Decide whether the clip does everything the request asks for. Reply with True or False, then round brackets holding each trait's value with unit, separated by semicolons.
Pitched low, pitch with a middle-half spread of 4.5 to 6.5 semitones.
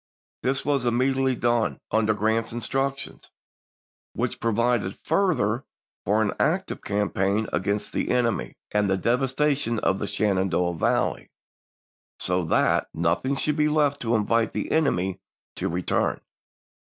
True (115 Hz; 5.0 semitones)